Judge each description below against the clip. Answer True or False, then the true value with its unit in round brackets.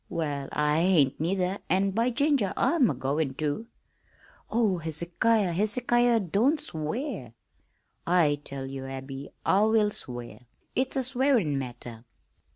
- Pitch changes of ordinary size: False (8.1 semitones)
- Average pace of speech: False (125 wpm)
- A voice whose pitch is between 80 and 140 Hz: False (180 Hz)